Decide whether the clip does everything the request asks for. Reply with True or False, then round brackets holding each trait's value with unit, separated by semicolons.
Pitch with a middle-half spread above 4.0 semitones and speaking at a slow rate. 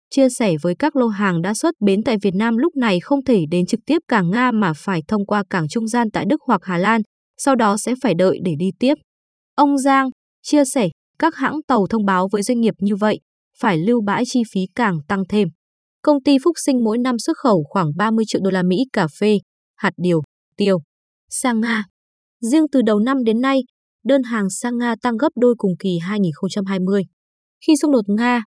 False (4.8 semitones; 220 wpm)